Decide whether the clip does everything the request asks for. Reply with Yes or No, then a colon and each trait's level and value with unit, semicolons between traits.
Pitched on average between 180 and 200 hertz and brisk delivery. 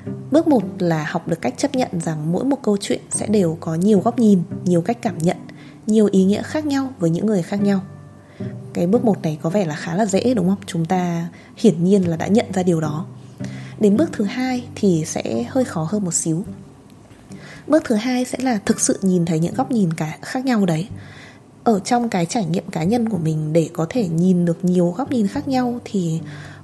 No: medium, 185 Hz; average, 230 wpm